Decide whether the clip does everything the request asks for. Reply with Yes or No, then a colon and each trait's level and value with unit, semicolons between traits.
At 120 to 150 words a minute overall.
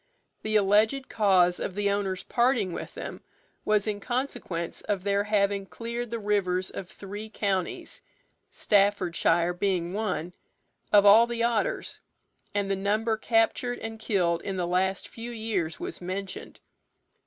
Yes: average, 140 wpm